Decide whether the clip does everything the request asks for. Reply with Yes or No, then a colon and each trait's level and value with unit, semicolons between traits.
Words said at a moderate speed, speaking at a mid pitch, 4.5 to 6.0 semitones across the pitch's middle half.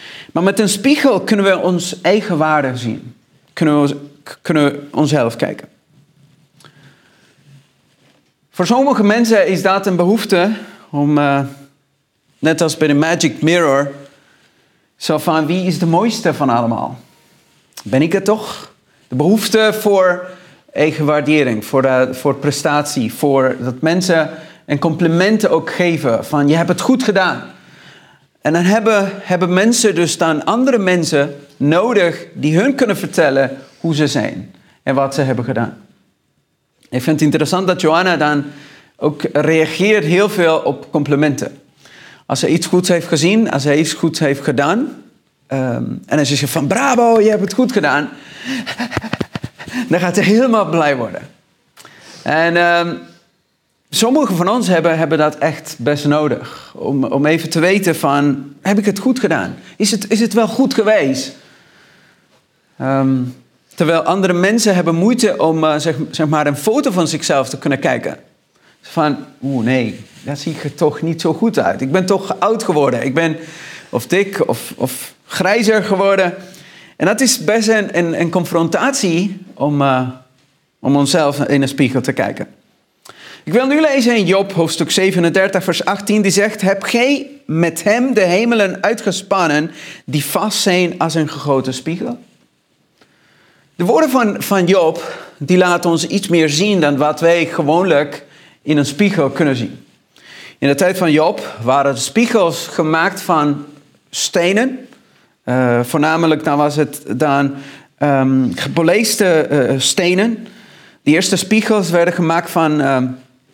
Yes: average, 155 wpm; medium, 165 Hz; average, 5.2 semitones